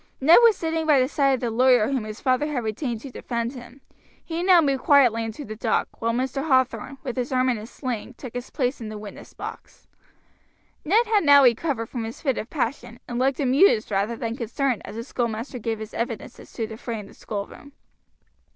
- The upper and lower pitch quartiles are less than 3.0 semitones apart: No, average, 3.4 semitones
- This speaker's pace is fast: Yes, fast, 220 wpm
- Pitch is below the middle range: No, very high, 250 Hz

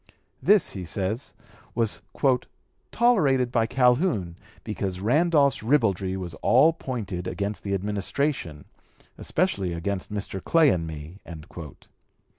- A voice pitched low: Yes, low, 105 Hz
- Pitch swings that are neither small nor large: No, wide, 6.9 semitones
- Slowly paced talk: Yes, slow, 105 wpm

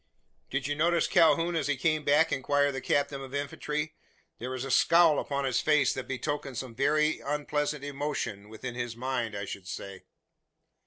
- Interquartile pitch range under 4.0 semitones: Yes, average, 2.8 semitones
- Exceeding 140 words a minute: Yes, average, 175 wpm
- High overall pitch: No, medium, 140 Hz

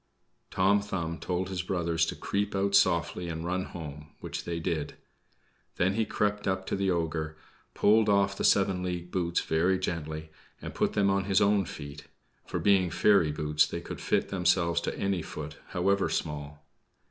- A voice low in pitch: Yes, very low, 90 Hz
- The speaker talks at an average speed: Yes, average, 175 wpm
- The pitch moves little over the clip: No, average, 3.3 semitones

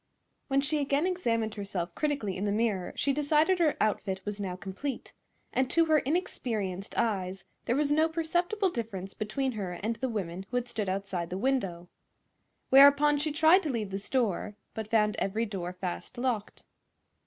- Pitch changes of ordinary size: No, wide, 6.7 semitones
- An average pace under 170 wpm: No, average, 175 wpm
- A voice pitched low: No, high, 230 Hz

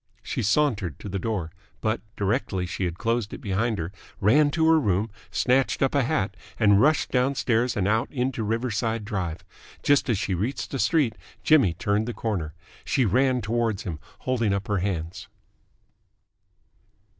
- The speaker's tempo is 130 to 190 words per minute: Yes, average, 165 wpm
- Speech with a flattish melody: No, average, 4.5 semitones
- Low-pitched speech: Yes, low, 110 Hz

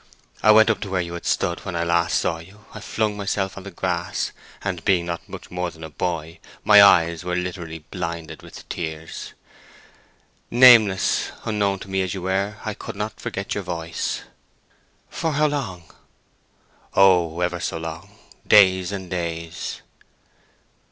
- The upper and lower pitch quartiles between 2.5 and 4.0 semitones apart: Yes, average, 2.9 semitones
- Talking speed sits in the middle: Yes, average, 150 wpm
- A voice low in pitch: Yes, very low, 90 Hz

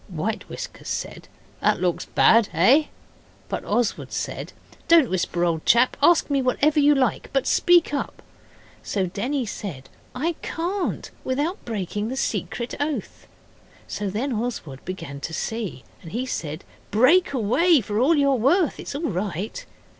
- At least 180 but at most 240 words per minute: No, average, 150 wpm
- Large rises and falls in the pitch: Yes, wide, 7.1 semitones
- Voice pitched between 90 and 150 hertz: No, high, 240 Hz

